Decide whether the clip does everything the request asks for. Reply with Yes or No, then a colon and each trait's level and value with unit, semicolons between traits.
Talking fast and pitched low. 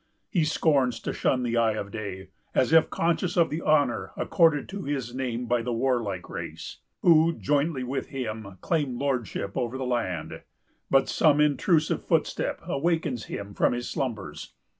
No: average, 160 wpm; low, 130 Hz